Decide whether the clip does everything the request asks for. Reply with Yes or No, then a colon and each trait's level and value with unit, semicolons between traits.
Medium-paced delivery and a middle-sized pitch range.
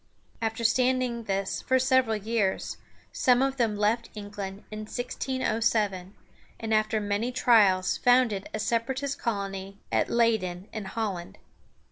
No: slow, 125 wpm; average, 3.5 semitones